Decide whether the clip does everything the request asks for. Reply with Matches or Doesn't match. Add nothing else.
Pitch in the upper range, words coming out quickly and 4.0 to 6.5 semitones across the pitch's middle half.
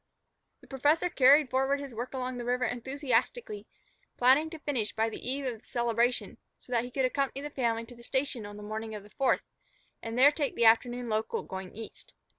Doesn't match